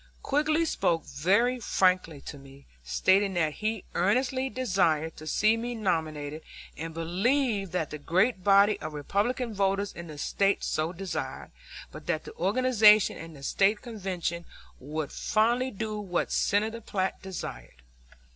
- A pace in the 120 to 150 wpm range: Yes, average, 145 wpm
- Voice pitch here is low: No, high, 195 Hz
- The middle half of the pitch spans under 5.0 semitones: No, average, 5.3 semitones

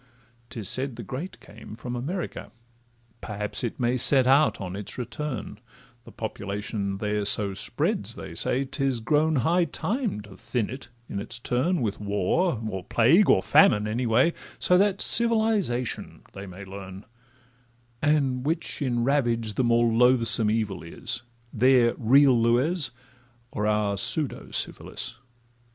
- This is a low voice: Yes, low, 120 Hz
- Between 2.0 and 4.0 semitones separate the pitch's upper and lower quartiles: No, average, 4.9 semitones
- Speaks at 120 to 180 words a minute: Yes, average, 145 wpm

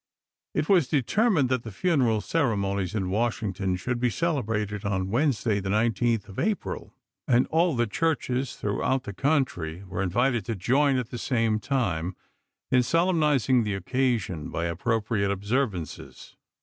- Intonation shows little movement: No, average, 5.1 semitones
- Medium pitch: No, low, 115 Hz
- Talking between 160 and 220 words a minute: No, average, 145 wpm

